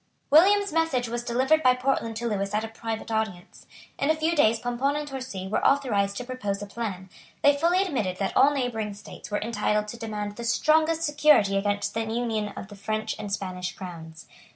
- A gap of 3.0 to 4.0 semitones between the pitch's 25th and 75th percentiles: No, average, 5.1 semitones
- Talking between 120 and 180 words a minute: No, average, 200 wpm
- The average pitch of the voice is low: No, high, 225 Hz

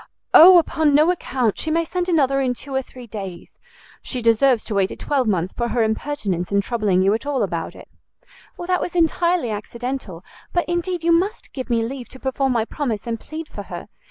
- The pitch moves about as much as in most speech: No, wide, 6.5 semitones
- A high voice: Yes, very high, 255 Hz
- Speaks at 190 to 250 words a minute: Yes, fast, 205 wpm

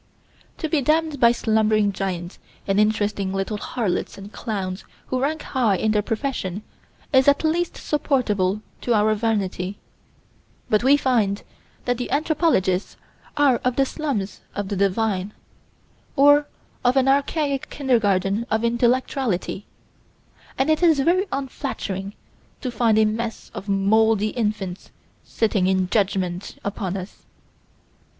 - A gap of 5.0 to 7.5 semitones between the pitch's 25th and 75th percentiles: Yes, average, 5.3 semitones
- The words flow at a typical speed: No, slow, 130 wpm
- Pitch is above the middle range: Yes, high, 220 Hz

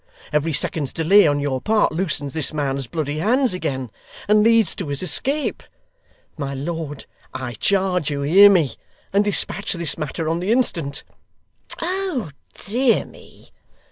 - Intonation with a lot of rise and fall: Yes, wide, 6.1 semitones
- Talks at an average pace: Yes, average, 145 wpm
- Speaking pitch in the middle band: Yes, medium, 165 Hz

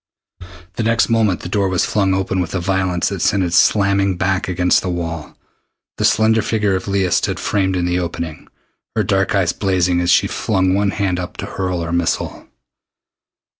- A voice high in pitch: No, very low, 95 Hz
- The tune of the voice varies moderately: No, narrow, 1.9 semitones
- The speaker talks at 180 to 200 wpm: Yes, average, 190 wpm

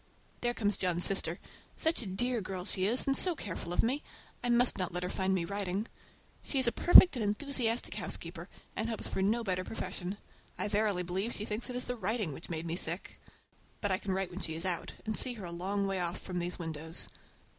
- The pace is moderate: No, fast, 230 wpm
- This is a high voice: Yes, high, 195 Hz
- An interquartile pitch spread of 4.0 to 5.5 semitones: Yes, average, 4.3 semitones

